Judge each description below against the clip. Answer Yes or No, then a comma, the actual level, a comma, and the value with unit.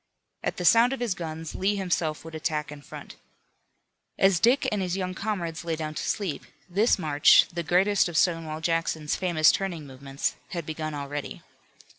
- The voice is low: No, medium, 165 Hz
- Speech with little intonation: No, average, 3.6 semitones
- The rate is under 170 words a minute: No, average, 175 wpm